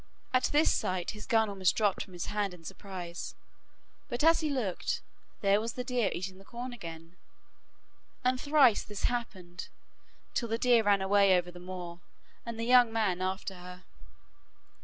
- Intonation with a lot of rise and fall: No, average, 4.7 semitones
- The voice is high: Yes, high, 200 Hz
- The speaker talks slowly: No, average, 170 wpm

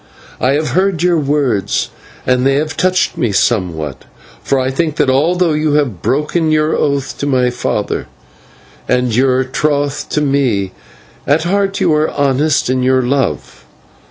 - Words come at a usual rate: Yes, average, 155 wpm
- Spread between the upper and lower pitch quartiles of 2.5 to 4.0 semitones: Yes, average, 3.3 semitones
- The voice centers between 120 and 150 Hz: Yes, medium, 140 Hz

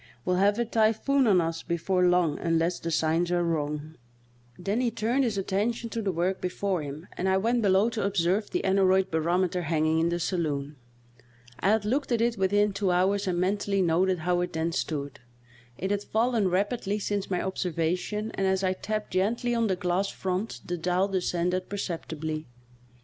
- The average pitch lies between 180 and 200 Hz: Yes, medium, 185 Hz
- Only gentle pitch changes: No, average, 3.2 semitones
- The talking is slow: No, average, 190 wpm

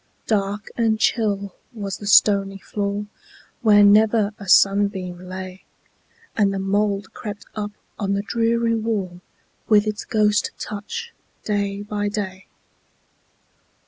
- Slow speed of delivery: Yes, slow, 110 wpm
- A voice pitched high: Yes, high, 205 Hz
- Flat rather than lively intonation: Yes, narrow, 1.4 semitones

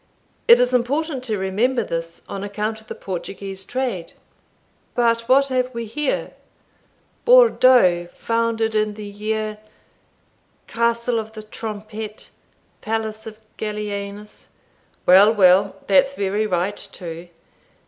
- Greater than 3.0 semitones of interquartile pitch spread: No, average, 2.7 semitones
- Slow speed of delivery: Yes, slow, 120 wpm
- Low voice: No, high, 215 Hz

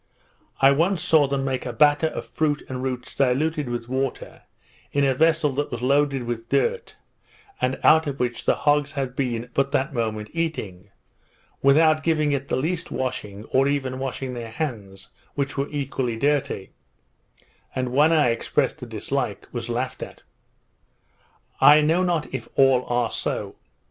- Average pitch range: Yes, average, 3.1 semitones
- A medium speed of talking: Yes, average, 165 wpm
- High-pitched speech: No, low, 135 Hz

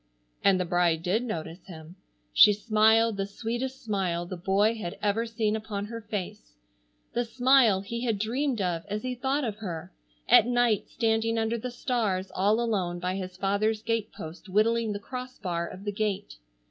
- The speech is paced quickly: No, average, 180 wpm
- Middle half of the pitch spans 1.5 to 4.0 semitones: Yes, average, 3.6 semitones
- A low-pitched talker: No, high, 210 Hz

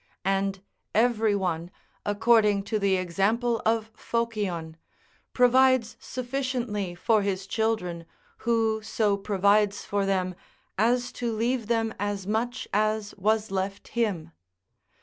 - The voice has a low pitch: No, high, 215 Hz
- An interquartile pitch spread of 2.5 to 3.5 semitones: Yes, average, 2.8 semitones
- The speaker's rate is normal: No, slow, 115 wpm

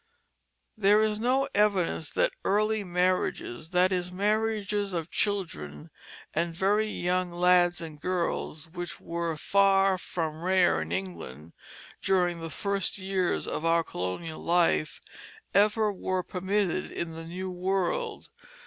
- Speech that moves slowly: Yes, slow, 130 wpm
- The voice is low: No, medium, 180 Hz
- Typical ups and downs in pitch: Yes, average, 3.1 semitones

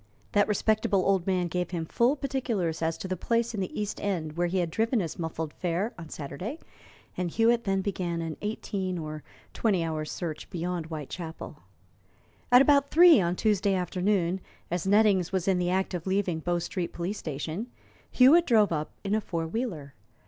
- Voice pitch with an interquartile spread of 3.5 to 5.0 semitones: Yes, average, 4.1 semitones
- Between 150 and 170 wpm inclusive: No, average, 185 wpm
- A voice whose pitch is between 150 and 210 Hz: Yes, medium, 185 Hz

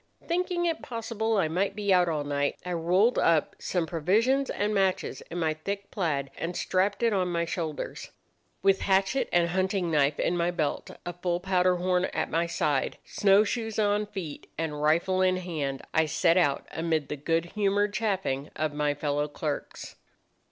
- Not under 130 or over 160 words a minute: No, average, 175 wpm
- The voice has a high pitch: No, medium, 180 Hz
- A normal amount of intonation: Yes, average, 4.1 semitones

